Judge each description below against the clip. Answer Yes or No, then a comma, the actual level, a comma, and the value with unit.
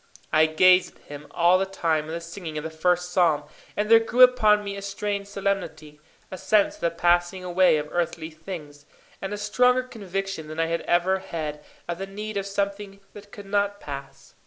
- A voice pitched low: No, medium, 185 Hz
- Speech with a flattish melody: No, average, 3.6 semitones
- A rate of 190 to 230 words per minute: Yes, fast, 205 wpm